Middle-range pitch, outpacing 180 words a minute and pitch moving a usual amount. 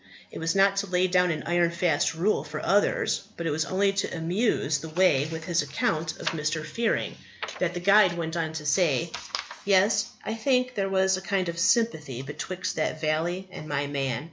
Yes: medium, 170 Hz; average, 200 wpm; average, 3.7 semitones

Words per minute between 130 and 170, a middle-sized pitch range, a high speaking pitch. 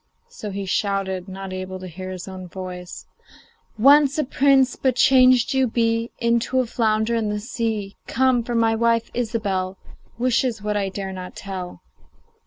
Yes: average, 165 wpm; average, 4.1 semitones; high, 220 Hz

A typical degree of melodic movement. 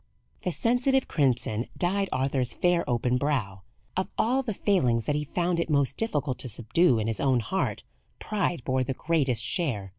No: wide, 6.6 semitones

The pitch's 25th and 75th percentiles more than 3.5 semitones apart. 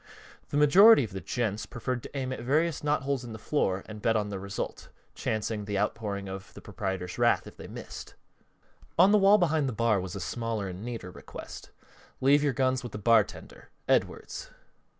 Yes: wide, 5.5 semitones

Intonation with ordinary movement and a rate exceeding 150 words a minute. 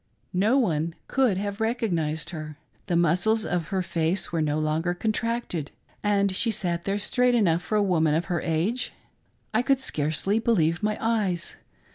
Yes: average, 4.9 semitones; average, 165 wpm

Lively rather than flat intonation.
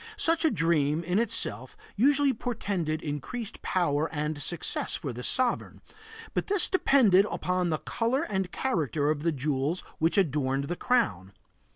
Yes: wide, 7.7 semitones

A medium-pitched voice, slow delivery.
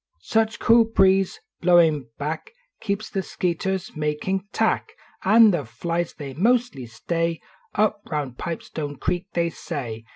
Yes: medium, 170 Hz; slow, 130 wpm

